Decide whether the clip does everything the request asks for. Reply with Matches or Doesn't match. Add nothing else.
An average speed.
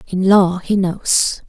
Matches